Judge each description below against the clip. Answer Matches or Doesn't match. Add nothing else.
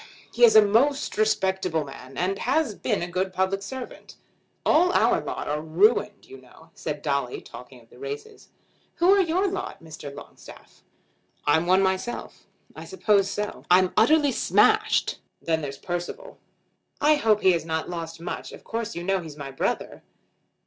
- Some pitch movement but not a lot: Doesn't match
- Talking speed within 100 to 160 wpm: Doesn't match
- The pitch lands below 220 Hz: Matches